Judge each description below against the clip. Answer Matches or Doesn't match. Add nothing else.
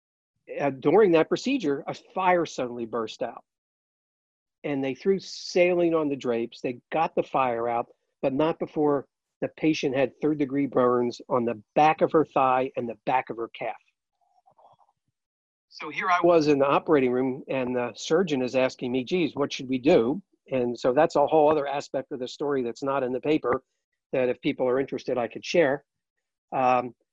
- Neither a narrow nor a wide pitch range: Matches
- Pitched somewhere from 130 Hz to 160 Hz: Matches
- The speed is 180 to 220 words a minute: Matches